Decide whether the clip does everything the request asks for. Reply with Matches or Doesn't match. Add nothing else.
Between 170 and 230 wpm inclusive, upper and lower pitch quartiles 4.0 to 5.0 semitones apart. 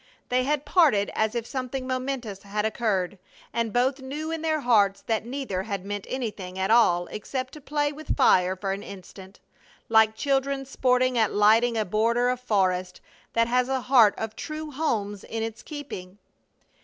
Matches